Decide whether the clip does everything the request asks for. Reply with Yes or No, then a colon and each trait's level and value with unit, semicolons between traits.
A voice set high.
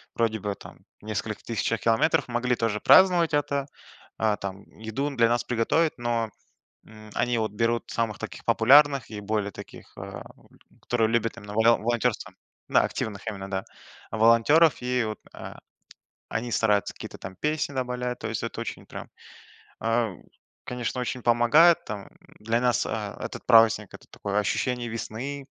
No: low, 115 Hz